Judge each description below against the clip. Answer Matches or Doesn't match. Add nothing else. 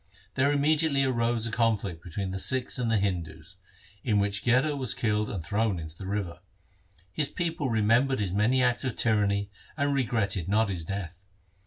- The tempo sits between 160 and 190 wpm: Matches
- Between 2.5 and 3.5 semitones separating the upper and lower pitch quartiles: Doesn't match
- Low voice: Matches